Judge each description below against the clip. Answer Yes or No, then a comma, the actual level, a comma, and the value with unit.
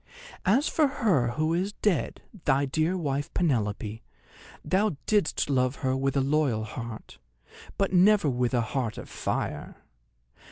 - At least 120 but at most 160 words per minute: Yes, average, 145 wpm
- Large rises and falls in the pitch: Yes, wide, 6.8 semitones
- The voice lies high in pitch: No, medium, 140 Hz